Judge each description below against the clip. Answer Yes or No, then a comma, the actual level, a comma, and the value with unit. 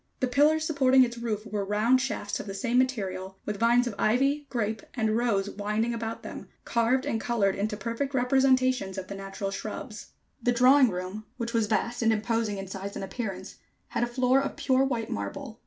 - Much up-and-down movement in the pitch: No, average, 3.9 semitones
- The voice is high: Yes, high, 230 Hz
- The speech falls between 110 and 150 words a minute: No, average, 195 wpm